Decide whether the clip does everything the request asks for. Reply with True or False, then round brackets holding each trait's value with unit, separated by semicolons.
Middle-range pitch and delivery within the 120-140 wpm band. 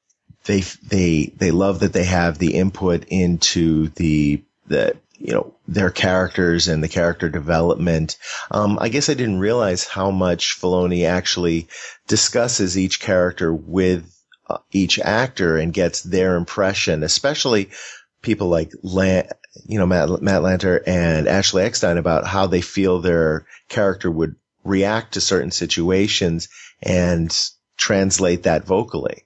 False (90 Hz; 135 wpm)